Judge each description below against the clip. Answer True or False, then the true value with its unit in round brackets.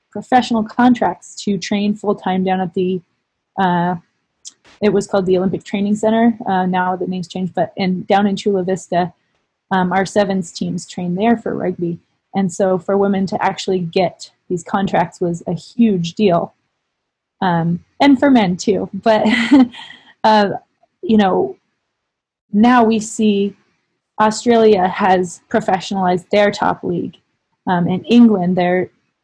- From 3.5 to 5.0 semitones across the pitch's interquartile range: False (2.9 semitones)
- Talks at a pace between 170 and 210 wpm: False (145 wpm)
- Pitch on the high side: True (195 Hz)